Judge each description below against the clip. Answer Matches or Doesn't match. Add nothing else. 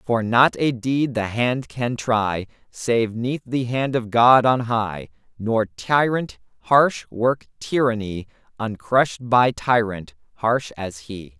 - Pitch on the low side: Matches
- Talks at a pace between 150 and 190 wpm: Doesn't match